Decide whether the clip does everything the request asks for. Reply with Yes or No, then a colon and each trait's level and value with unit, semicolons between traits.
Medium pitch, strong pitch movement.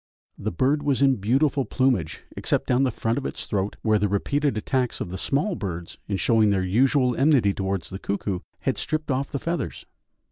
No: low, 125 Hz; wide, 5.7 semitones